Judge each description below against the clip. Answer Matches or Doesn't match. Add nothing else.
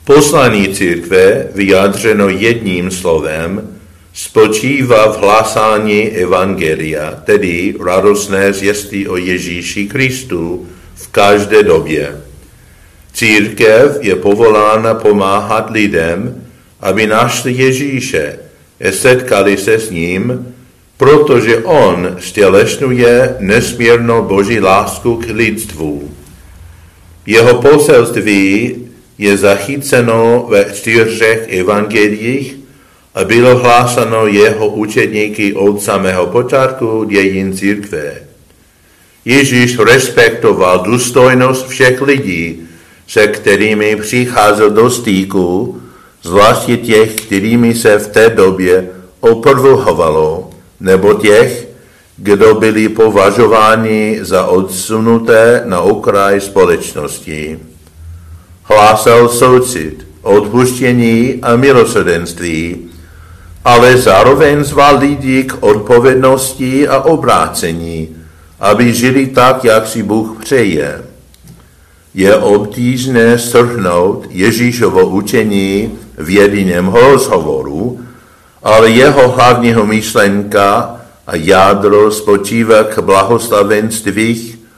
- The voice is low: Matches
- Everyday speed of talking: Doesn't match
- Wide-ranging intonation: Doesn't match